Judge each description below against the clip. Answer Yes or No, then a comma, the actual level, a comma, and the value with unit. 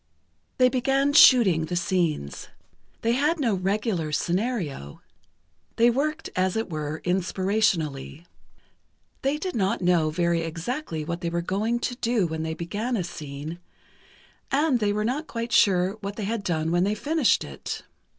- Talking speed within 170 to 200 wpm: No, average, 155 wpm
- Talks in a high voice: Yes, high, 195 Hz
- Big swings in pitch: Yes, wide, 6.0 semitones